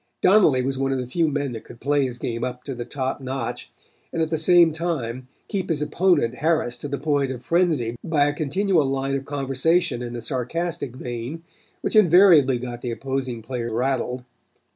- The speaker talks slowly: No, average, 195 wpm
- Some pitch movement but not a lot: Yes, average, 4.4 semitones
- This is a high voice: No, low, 135 Hz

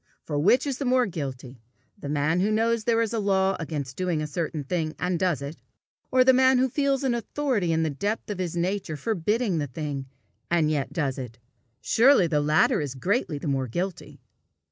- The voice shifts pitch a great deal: Yes, wide, 7.4 semitones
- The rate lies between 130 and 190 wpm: No, fast, 205 wpm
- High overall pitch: No, medium, 175 Hz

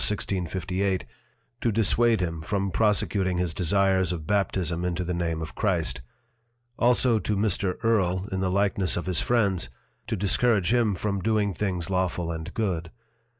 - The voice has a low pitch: Yes, very low, 95 Hz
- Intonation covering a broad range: No, average, 2.8 semitones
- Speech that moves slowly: No, average, 150 wpm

